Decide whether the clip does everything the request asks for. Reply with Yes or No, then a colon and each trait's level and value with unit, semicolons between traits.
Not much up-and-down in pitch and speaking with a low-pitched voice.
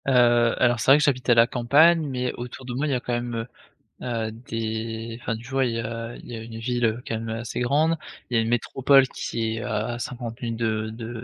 Yes: narrow, 1.8 semitones; low, 120 Hz